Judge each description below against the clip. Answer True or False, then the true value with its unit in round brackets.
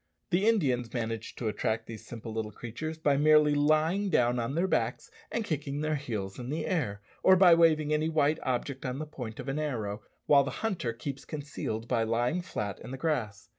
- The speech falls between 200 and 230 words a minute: True (205 wpm)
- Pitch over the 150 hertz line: False (140 Hz)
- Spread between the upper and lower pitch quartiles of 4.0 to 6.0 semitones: True (5.0 semitones)